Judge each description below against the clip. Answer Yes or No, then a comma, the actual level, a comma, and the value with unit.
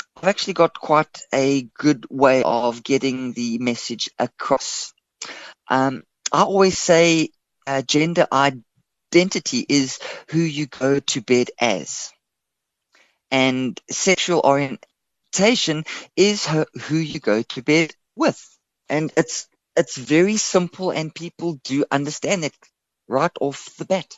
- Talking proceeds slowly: Yes, slow, 125 wpm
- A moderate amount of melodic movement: Yes, average, 4.3 semitones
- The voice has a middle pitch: Yes, medium, 150 Hz